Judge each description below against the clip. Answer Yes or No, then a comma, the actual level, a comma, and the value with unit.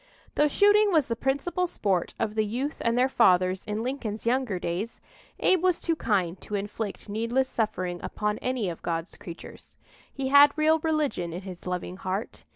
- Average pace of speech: Yes, average, 175 wpm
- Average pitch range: No, wide, 6.9 semitones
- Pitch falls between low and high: No, high, 225 Hz